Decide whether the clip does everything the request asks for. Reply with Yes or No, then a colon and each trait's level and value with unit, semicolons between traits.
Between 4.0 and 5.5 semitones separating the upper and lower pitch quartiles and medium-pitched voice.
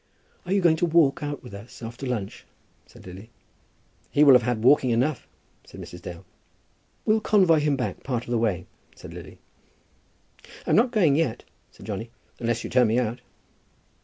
No: average, 5.2 semitones; low, 125 Hz